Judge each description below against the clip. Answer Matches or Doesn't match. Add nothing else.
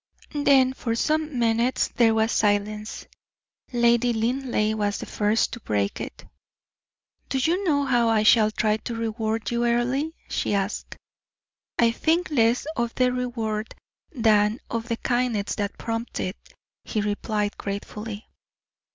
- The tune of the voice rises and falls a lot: Doesn't match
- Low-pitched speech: Doesn't match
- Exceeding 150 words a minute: Doesn't match